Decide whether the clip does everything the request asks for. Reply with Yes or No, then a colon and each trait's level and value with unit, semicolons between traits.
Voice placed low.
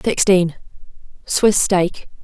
No: medium, 185 Hz